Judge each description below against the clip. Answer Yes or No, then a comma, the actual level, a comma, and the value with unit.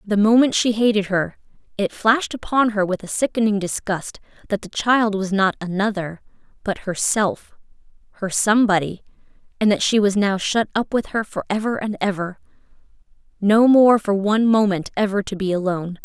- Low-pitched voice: No, high, 205 Hz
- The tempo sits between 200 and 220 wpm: No, average, 170 wpm